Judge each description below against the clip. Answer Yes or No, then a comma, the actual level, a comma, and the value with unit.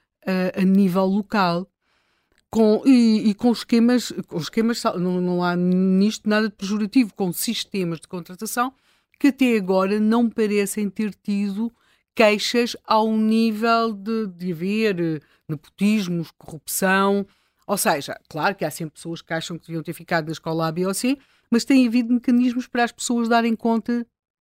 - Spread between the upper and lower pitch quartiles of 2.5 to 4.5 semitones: Yes, average, 4.2 semitones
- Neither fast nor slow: Yes, average, 160 wpm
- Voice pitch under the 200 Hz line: No, high, 210 Hz